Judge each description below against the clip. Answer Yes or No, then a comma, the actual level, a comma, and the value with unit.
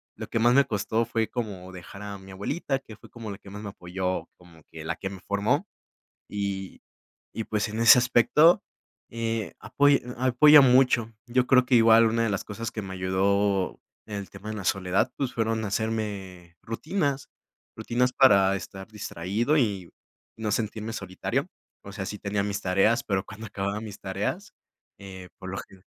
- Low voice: Yes, low, 105 Hz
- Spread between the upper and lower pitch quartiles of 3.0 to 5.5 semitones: Yes, average, 3.3 semitones